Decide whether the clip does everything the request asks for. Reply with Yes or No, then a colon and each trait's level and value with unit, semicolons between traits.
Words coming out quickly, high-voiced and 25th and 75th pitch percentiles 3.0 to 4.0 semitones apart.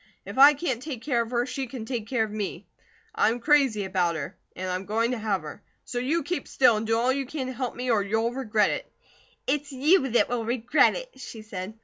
Yes: fast, 245 wpm; high, 240 Hz; average, 3.7 semitones